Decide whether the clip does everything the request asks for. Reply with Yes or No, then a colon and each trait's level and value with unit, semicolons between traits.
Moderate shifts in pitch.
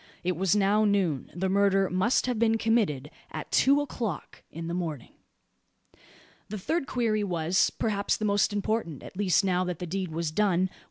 Yes: average, 3.5 semitones